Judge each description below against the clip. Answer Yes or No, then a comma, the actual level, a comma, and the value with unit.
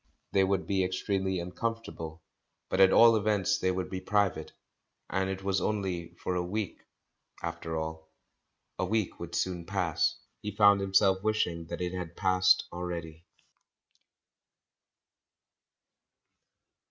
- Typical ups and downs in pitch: No, narrow, 2.3 semitones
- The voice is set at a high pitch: No, very low, 95 Hz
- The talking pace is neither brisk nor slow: No, slow, 130 wpm